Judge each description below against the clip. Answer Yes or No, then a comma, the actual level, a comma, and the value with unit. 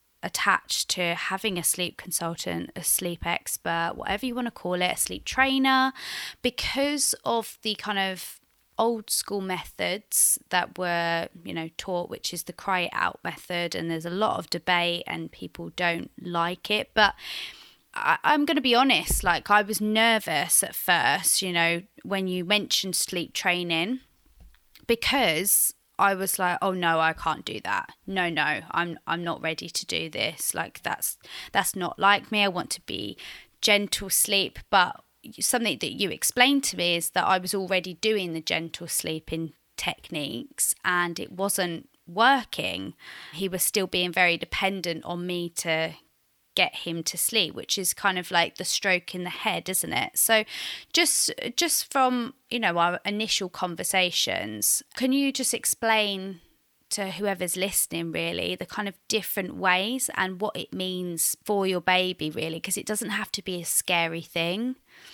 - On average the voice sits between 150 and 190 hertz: Yes, medium, 185 Hz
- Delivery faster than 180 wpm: No, average, 170 wpm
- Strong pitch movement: No, average, 3.8 semitones